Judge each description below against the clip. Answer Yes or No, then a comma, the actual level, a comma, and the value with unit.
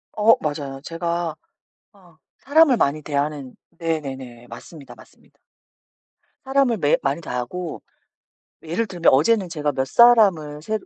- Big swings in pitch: Yes, wide, 6.0 semitones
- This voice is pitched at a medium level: Yes, medium, 160 Hz